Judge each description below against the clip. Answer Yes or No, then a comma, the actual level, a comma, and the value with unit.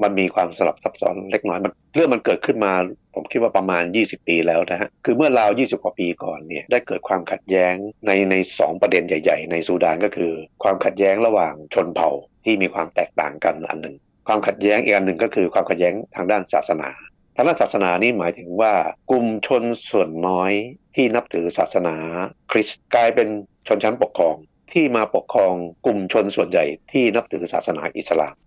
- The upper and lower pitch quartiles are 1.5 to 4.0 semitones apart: Yes, average, 3.6 semitones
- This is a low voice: Yes, very low, 95 Hz